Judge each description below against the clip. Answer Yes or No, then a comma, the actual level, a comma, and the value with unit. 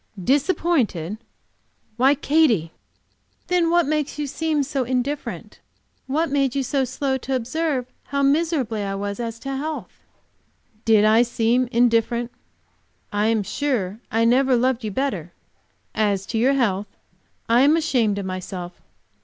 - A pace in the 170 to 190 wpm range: No, average, 145 wpm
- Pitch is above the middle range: Yes, very high, 250 Hz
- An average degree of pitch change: Yes, average, 4.5 semitones